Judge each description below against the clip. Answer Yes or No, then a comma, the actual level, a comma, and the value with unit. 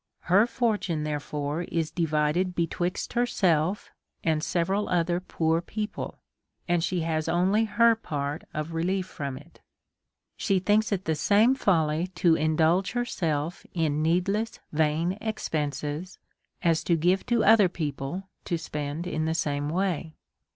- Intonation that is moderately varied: Yes, average, 3.7 semitones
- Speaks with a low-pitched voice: No, medium, 170 Hz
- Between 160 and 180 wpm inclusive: No, average, 140 wpm